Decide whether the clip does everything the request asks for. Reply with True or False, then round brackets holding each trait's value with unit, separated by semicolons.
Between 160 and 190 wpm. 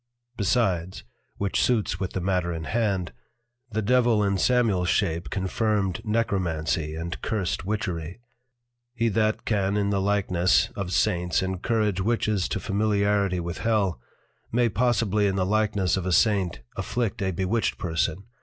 False (145 wpm)